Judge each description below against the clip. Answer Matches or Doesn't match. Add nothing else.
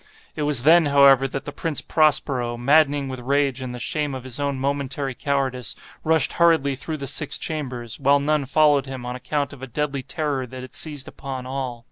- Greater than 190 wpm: Matches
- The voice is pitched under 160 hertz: Matches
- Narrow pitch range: Matches